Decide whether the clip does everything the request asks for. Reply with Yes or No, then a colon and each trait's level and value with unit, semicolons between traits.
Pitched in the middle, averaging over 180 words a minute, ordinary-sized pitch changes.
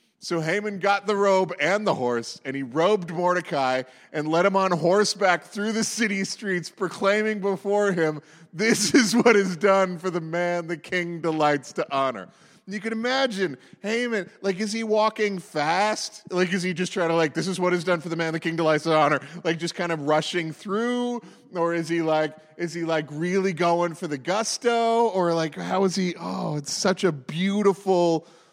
Yes: medium, 180 Hz; average, 200 wpm; average, 3.5 semitones